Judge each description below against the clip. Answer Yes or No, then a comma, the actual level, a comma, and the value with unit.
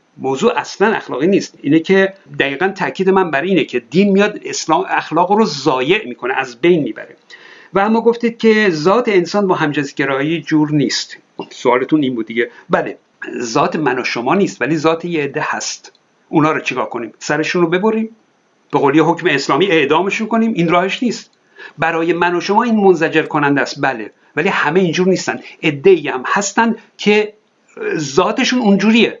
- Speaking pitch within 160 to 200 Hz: Yes, medium, 185 Hz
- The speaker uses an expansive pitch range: Yes, wide, 5.9 semitones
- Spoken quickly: Yes, fast, 170 wpm